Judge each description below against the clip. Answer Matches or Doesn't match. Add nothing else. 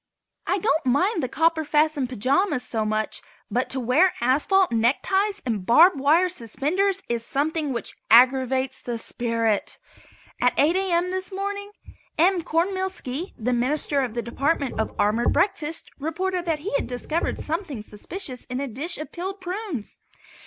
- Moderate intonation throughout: Doesn't match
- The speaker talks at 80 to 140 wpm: Doesn't match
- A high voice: Matches